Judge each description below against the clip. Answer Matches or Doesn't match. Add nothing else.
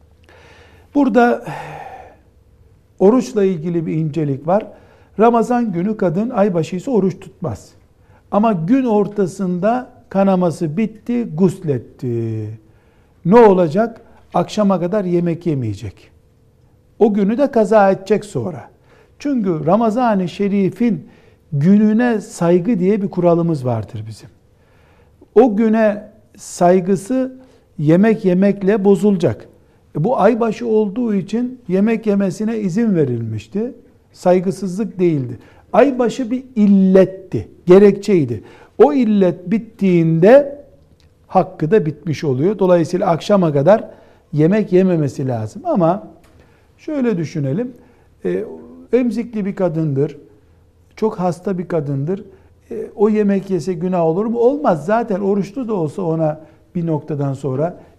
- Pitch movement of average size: Doesn't match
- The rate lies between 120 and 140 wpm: Doesn't match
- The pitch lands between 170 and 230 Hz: Matches